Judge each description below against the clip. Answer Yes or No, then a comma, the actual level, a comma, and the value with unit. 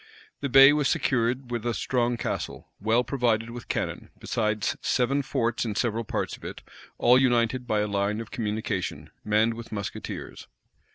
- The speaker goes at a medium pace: Yes, average, 165 wpm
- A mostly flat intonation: Yes, narrow, 2.3 semitones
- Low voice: Yes, low, 115 Hz